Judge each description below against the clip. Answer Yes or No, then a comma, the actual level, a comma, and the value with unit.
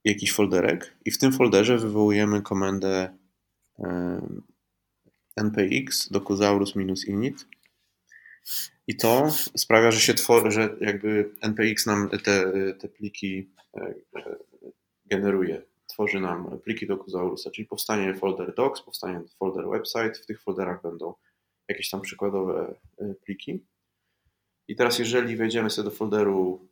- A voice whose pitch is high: No, low, 100 Hz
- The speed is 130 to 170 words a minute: No, slow, 110 wpm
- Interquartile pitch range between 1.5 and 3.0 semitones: Yes, narrow, 2.4 semitones